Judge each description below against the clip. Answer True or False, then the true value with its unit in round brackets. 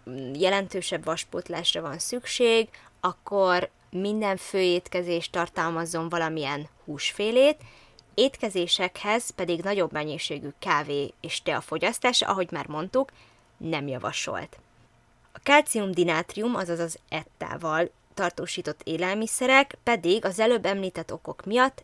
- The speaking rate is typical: False (100 wpm)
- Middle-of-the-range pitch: True (180 Hz)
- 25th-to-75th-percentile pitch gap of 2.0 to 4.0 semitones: False (4.8 semitones)